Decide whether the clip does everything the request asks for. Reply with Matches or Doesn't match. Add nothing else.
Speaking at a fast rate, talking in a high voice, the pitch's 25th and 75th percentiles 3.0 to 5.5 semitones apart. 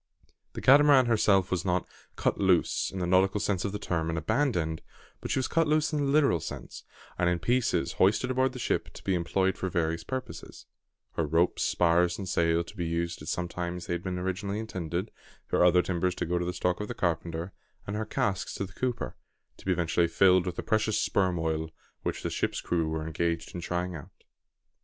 Doesn't match